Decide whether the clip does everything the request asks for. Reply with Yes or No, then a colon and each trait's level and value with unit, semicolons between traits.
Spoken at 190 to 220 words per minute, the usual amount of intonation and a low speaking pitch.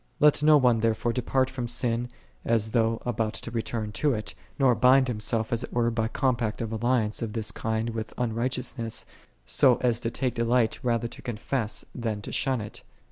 No: average, 195 wpm; narrow, 2.0 semitones; low, 115 Hz